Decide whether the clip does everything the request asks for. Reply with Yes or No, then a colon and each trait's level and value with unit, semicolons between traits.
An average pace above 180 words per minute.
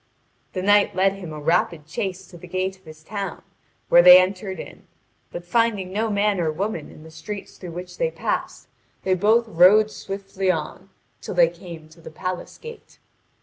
Yes: average, 190 wpm